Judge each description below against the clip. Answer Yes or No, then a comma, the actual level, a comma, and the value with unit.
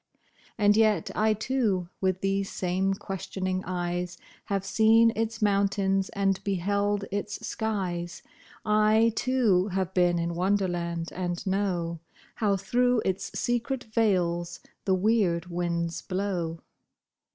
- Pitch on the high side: Yes, high, 195 Hz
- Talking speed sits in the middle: No, slow, 120 wpm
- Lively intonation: No, average, 3.1 semitones